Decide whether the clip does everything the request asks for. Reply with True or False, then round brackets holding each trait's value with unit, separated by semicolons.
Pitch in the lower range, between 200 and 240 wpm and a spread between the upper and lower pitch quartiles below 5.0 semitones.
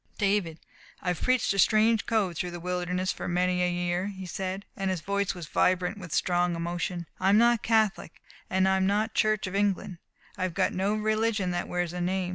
False (185 Hz; 205 wpm; 2.4 semitones)